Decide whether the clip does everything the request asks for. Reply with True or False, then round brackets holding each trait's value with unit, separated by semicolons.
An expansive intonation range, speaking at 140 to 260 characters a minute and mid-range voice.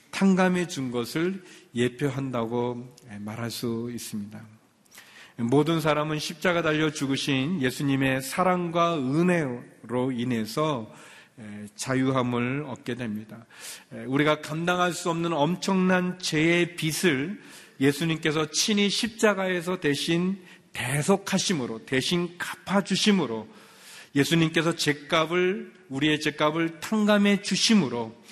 True (6.2 semitones; 250 characters per minute; 155 Hz)